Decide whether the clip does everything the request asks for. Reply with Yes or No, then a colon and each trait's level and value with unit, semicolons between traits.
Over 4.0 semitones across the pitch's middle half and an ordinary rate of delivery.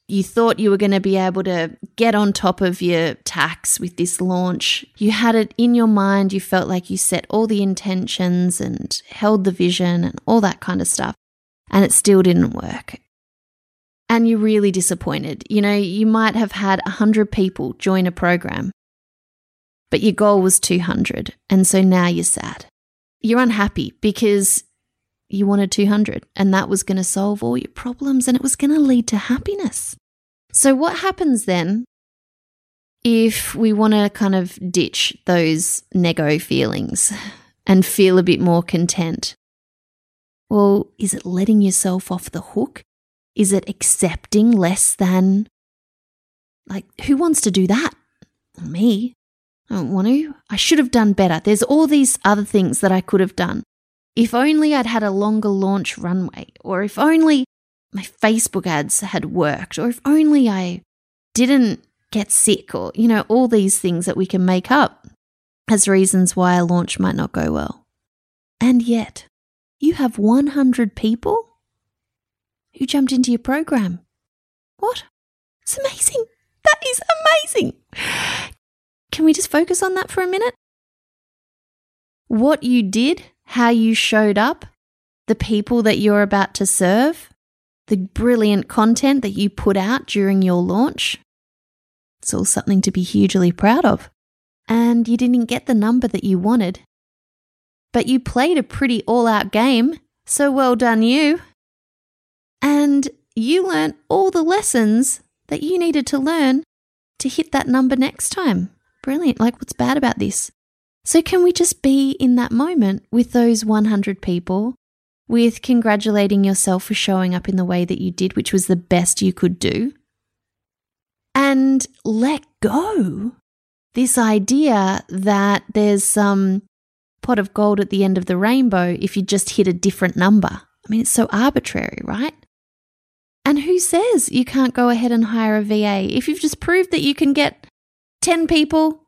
Yes: average, 5.1 semitones; average, 165 wpm